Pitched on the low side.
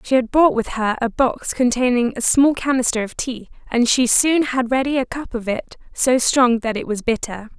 No: high, 245 Hz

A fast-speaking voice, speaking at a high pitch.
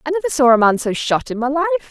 Yes: fast, 315 wpm; very high, 285 Hz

